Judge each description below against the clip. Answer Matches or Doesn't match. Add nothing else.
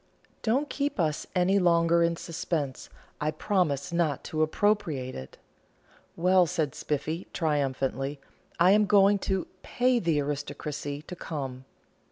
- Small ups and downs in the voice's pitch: Doesn't match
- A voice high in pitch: Doesn't match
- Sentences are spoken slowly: Matches